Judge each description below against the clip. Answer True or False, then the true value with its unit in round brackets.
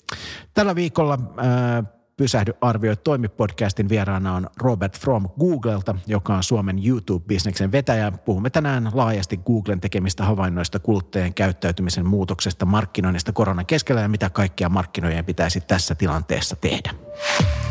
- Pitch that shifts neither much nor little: True (3.9 semitones)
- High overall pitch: False (105 Hz)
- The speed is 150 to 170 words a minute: False (120 wpm)